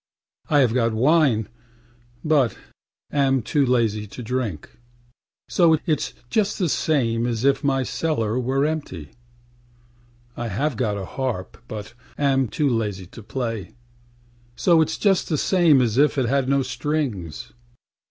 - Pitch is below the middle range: Yes, low, 130 Hz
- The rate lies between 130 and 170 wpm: Yes, average, 145 wpm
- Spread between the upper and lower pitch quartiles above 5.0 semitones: No, average, 4.6 semitones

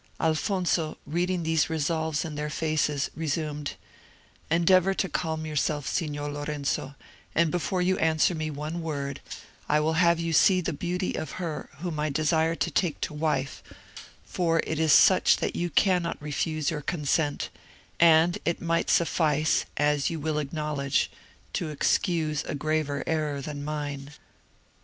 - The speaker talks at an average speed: Yes, average, 150 wpm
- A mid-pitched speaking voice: Yes, medium, 155 Hz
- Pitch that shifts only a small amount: Yes, narrow, 2.0 semitones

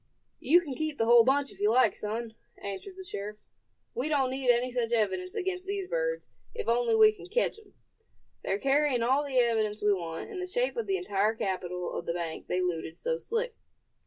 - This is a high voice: Yes, high, 245 Hz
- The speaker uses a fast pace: Yes, fast, 210 wpm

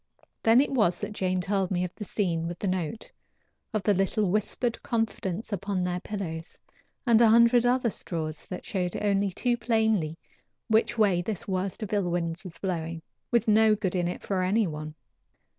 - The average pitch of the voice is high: Yes, high, 195 Hz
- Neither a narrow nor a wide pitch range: Yes, average, 3.8 semitones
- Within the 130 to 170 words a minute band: No, average, 185 wpm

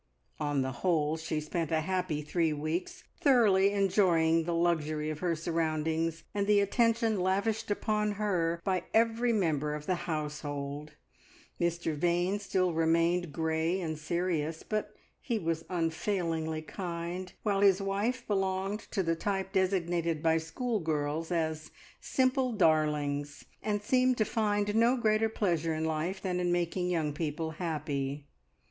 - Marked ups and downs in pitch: No, average, 4.0 semitones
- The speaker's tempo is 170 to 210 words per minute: No, average, 140 wpm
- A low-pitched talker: No, medium, 170 Hz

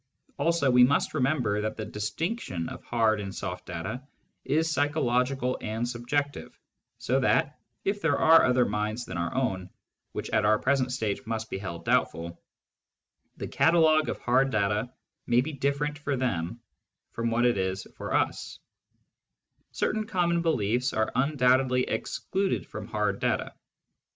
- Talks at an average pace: Yes, average, 155 wpm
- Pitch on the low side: Yes, low, 125 Hz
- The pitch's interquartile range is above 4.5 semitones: Yes, average, 5.0 semitones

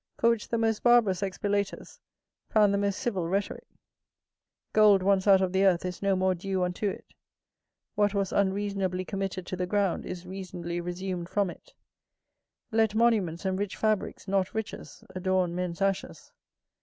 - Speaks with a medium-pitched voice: No, high, 195 Hz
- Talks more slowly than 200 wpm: Yes, average, 160 wpm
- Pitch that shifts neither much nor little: No, narrow, 1.8 semitones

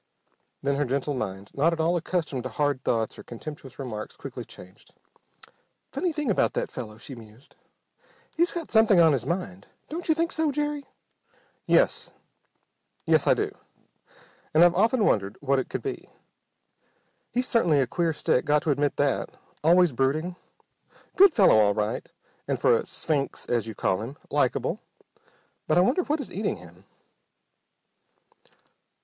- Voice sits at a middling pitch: Yes, medium, 150 Hz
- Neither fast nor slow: Yes, average, 160 wpm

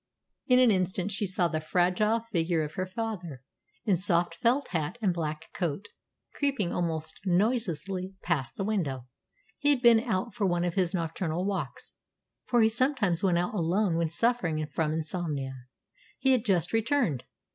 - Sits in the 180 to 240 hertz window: Yes, medium, 185 Hz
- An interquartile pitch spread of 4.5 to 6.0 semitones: Yes, average, 5.0 semitones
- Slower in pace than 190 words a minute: Yes, average, 165 wpm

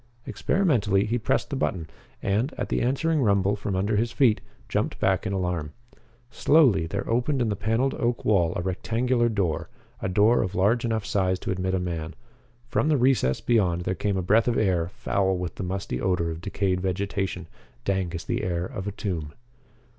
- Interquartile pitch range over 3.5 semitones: Yes, average, 4.2 semitones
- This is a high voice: No, low, 100 Hz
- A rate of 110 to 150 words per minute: No, average, 190 wpm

